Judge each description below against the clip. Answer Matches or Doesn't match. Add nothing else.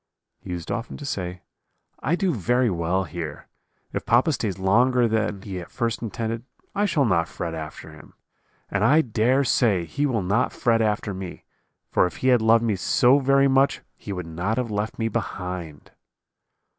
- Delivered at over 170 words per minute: Matches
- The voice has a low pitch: Matches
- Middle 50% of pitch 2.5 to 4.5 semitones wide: Doesn't match